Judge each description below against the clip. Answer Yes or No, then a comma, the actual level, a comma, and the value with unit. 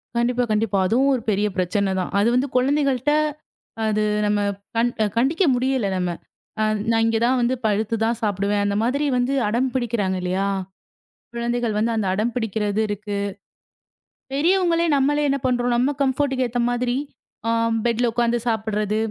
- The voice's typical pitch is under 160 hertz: No, high, 235 Hz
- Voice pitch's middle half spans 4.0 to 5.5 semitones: No, average, 3.5 semitones